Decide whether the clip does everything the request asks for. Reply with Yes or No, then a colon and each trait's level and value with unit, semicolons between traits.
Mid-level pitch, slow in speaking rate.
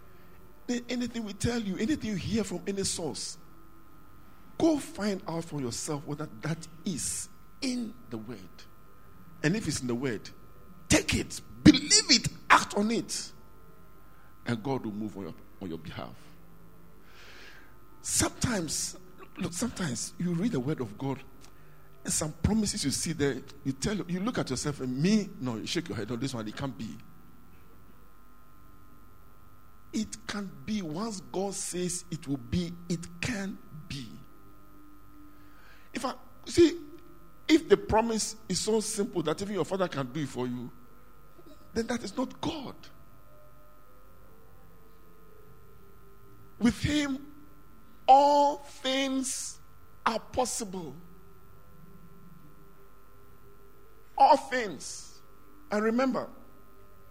Yes: medium, 155 Hz; slow, 130 wpm